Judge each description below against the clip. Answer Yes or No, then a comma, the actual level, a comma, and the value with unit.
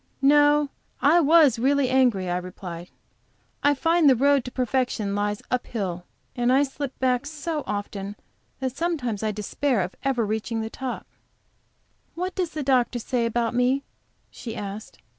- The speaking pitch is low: No, very high, 250 Hz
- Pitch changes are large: No, average, 4.9 semitones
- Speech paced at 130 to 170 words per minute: Yes, average, 160 wpm